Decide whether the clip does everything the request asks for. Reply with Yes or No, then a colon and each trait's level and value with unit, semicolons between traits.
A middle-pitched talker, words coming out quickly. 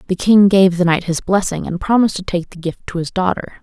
Yes: medium, 180 Hz; fast, 265 wpm